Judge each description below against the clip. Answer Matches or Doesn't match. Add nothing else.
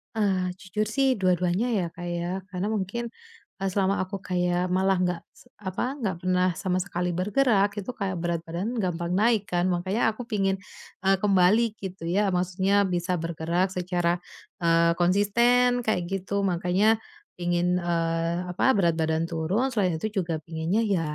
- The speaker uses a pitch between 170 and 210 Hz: Matches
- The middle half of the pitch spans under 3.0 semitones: Matches